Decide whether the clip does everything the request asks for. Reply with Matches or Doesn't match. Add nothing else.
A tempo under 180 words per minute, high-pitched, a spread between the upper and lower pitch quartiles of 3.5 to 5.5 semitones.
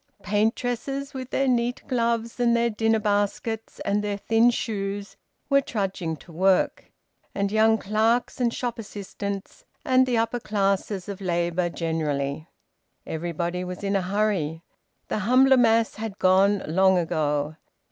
Matches